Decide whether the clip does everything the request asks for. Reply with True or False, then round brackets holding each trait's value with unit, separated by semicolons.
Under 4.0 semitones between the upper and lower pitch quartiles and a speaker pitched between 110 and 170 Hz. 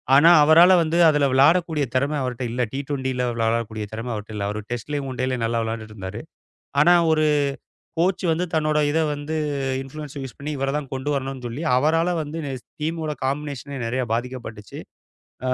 False (4.3 semitones; 135 Hz)